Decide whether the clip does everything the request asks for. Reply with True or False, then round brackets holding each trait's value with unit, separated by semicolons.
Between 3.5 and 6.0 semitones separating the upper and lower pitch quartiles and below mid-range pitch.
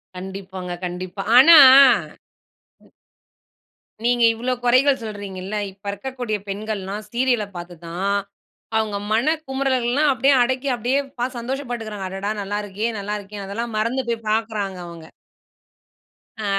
False (4.0 semitones; 215 Hz)